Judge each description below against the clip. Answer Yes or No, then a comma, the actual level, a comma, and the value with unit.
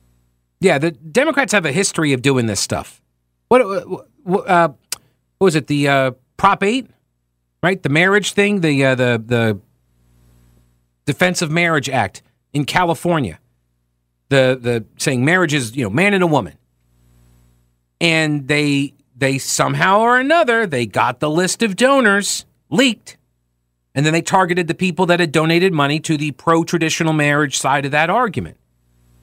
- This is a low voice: No, medium, 145 Hz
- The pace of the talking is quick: No, average, 155 wpm